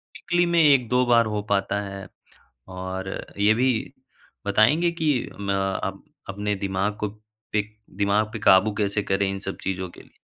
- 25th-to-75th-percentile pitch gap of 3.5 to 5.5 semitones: No, average, 3.0 semitones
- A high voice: No, low, 100 Hz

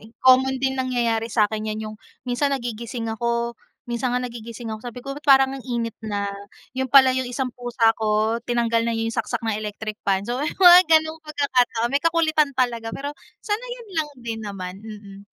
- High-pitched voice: Yes, high, 240 Hz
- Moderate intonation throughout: Yes, average, 3.0 semitones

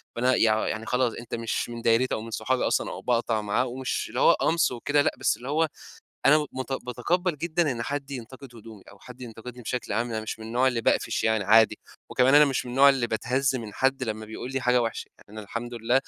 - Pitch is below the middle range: Yes, low, 125 Hz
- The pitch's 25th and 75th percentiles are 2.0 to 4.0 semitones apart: Yes, average, 2.7 semitones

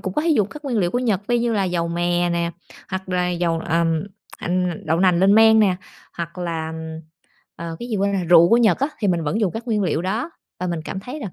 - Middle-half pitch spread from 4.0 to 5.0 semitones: Yes, average, 4.3 semitones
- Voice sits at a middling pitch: Yes, medium, 180 Hz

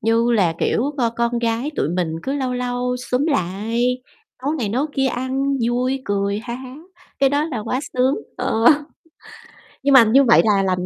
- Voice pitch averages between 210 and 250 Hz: Yes, high, 245 Hz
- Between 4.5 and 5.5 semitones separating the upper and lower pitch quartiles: No, average, 3.2 semitones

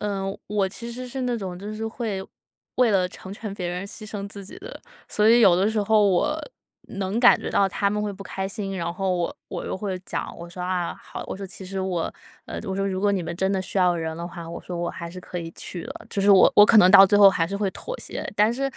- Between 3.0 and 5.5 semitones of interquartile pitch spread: No, narrow, 2.4 semitones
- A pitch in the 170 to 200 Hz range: Yes, high, 195 Hz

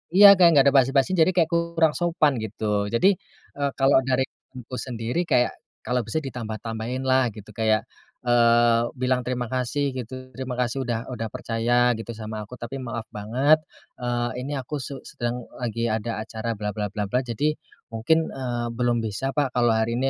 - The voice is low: Yes, low, 125 Hz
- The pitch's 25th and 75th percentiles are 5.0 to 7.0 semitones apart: No, average, 2.9 semitones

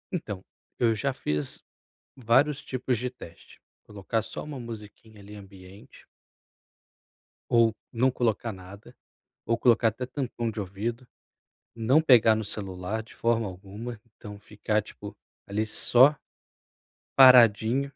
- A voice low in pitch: Yes, low, 115 Hz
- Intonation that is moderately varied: Yes, average, 3.1 semitones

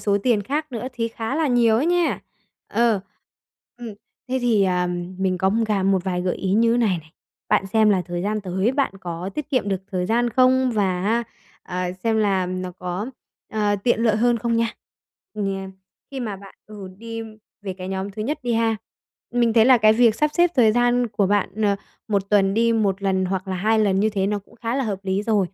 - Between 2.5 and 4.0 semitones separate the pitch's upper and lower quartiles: Yes, average, 3.5 semitones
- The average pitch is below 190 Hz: No, high, 210 Hz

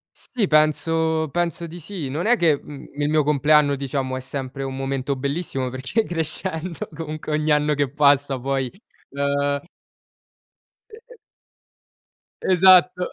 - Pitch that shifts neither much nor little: Yes, average, 3.0 semitones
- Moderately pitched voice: Yes, medium, 150 Hz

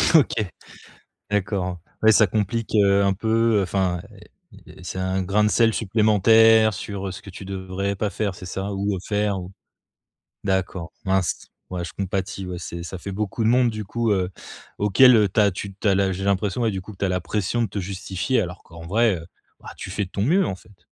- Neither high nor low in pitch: No, low, 100 Hz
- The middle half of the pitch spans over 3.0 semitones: No, narrow, 2.4 semitones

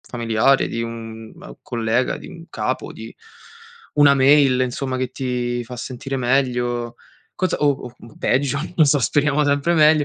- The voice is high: No, low, 130 Hz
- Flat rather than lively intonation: No, average, 3.0 semitones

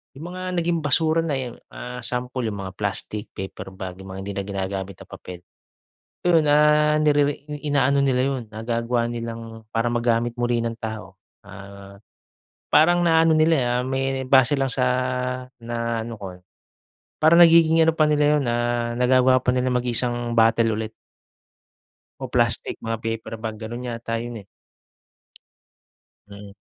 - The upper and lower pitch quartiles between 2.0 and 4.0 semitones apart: No, average, 4.5 semitones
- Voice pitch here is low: Yes, low, 120 Hz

